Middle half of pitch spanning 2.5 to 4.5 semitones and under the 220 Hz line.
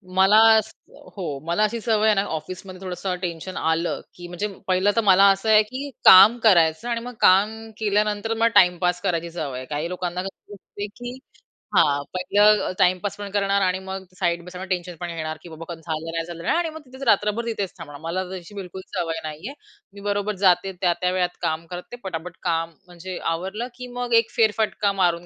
Yes: average, 3.3 semitones; medium, 185 Hz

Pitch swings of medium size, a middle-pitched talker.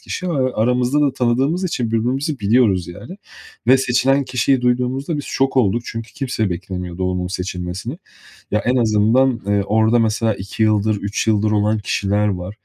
No: average, 4.1 semitones; low, 115 Hz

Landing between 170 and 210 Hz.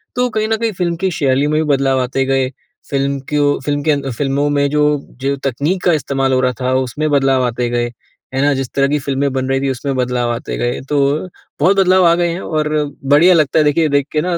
No: medium, 140 Hz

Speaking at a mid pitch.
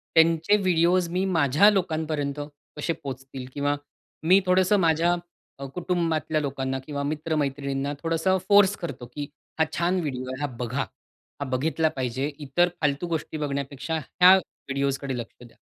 Yes: medium, 155 Hz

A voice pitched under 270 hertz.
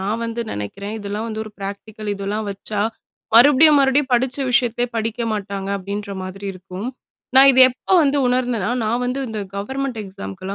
Yes: high, 220 Hz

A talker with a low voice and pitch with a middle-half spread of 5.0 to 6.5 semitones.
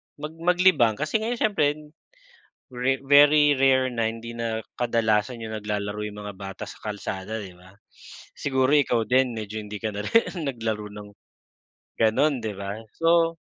Yes: low, 115 Hz; average, 5.3 semitones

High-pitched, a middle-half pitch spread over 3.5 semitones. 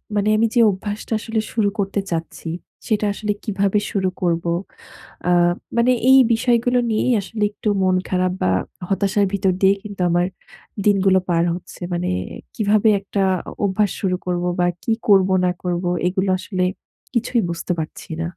No: high, 195 Hz; average, 2.8 semitones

